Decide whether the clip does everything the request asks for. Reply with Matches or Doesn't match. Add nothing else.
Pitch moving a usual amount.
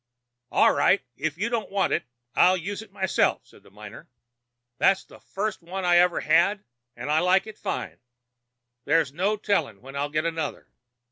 Matches